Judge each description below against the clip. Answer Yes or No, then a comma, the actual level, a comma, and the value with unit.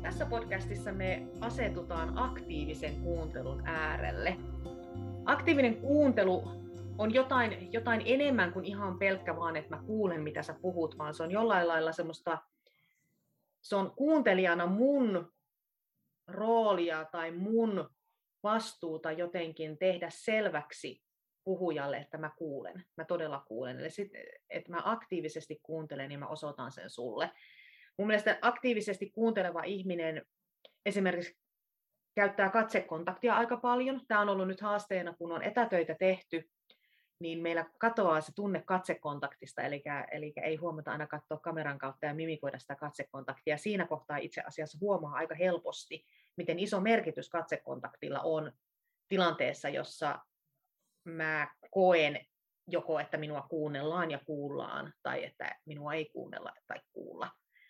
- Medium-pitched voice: Yes, medium, 170 Hz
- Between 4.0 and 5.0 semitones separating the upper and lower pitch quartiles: Yes, average, 4.7 semitones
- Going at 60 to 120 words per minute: No, average, 130 wpm